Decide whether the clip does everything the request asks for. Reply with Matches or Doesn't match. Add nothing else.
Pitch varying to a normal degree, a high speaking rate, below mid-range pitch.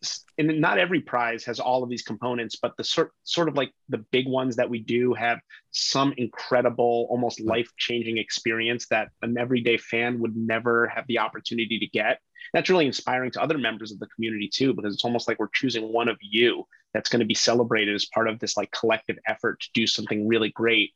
Doesn't match